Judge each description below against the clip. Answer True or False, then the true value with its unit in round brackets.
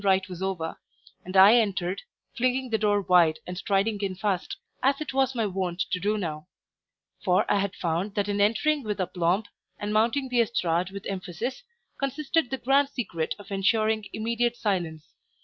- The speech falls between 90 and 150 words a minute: False (175 wpm)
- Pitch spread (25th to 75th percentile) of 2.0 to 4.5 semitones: True (4.2 semitones)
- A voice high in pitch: True (205 Hz)